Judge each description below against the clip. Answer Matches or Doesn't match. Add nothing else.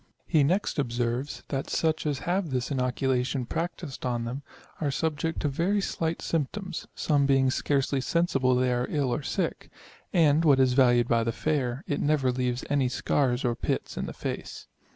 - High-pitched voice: Doesn't match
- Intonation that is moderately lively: Matches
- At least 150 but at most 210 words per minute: Matches